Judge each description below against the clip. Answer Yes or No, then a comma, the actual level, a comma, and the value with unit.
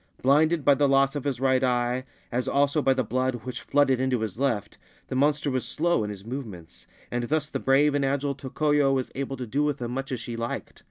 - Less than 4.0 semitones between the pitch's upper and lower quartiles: Yes, narrow, 2.5 semitones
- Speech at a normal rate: No, fast, 230 wpm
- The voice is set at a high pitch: No, low, 135 Hz